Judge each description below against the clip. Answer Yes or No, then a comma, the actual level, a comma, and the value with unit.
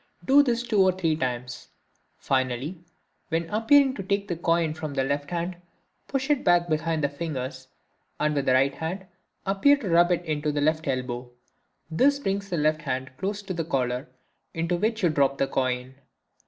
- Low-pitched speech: No, medium, 160 Hz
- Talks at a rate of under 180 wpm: No, average, 185 wpm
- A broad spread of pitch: Yes, wide, 5.9 semitones